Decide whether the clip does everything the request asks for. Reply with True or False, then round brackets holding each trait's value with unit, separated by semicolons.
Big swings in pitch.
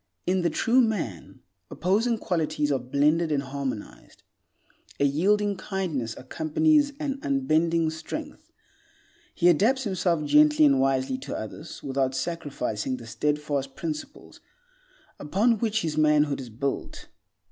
True (5.8 semitones)